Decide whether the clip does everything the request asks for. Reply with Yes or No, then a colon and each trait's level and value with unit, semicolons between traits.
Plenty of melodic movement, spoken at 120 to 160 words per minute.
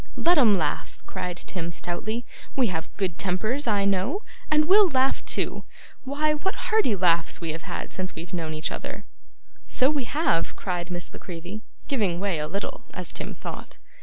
No: wide, 7.7 semitones; average, 180 wpm